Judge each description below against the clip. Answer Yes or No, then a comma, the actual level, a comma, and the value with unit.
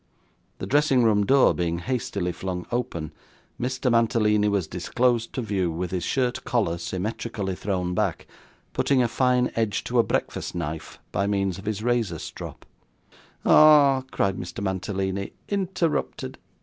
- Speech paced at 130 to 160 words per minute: Yes, average, 145 wpm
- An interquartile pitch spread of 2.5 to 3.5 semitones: No, average, 5.1 semitones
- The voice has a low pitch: Yes, low, 105 Hz